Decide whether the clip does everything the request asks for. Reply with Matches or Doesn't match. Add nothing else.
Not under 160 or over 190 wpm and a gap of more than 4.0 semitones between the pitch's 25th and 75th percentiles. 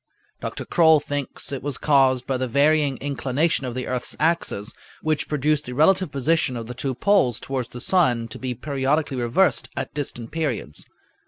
Doesn't match